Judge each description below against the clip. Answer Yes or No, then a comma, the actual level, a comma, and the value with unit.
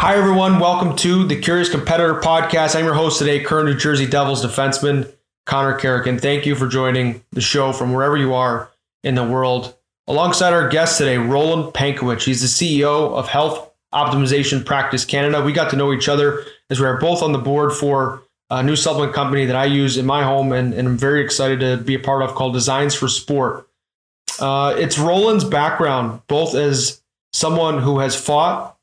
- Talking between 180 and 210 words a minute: Yes, average, 200 wpm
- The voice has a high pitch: No, medium, 140 Hz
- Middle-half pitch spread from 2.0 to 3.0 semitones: Yes, narrow, 2.6 semitones